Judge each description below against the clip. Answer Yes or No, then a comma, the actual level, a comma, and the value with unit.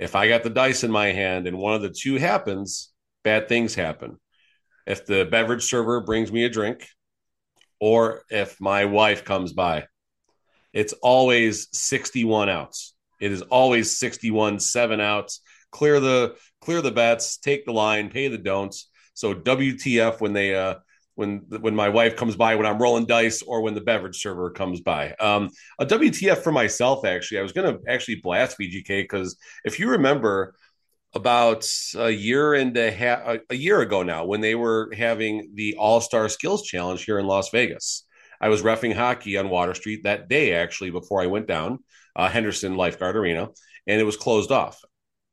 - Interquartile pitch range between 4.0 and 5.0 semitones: No, average, 2.8 semitones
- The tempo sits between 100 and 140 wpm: No, average, 180 wpm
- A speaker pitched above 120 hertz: No, low, 110 Hz